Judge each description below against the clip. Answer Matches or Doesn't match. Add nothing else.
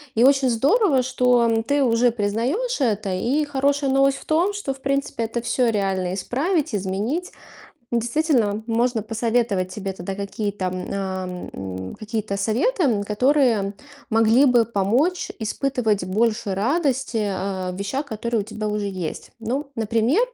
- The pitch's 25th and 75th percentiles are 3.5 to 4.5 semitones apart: Doesn't match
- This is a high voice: Matches